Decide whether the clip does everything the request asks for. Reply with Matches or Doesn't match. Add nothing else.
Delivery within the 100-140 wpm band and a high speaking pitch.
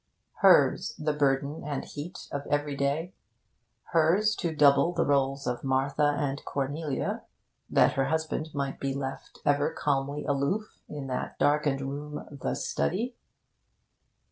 Doesn't match